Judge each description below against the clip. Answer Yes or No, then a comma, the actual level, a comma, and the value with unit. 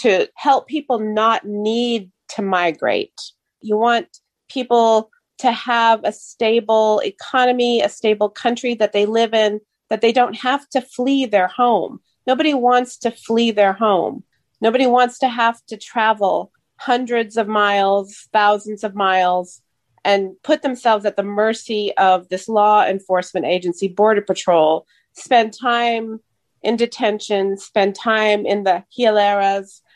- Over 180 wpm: No, average, 140 wpm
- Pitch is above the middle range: Yes, high, 220 Hz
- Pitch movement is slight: No, average, 3.0 semitones